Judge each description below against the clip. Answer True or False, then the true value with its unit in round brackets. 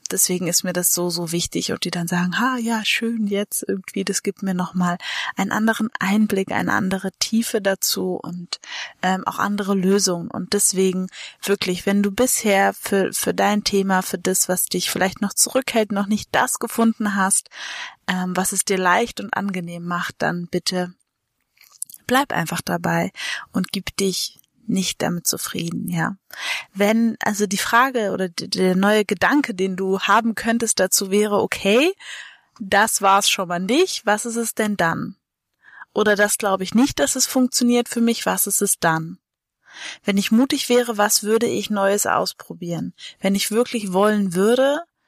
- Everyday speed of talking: True (170 wpm)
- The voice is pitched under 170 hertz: False (200 Hz)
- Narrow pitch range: False (3.3 semitones)